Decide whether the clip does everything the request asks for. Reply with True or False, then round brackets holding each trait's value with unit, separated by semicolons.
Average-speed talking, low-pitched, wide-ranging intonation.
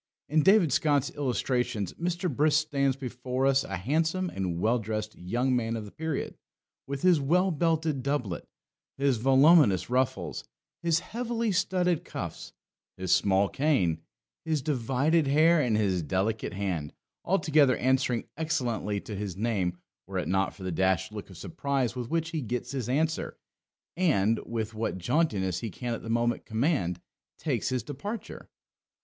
True (155 wpm; 130 Hz; 6.5 semitones)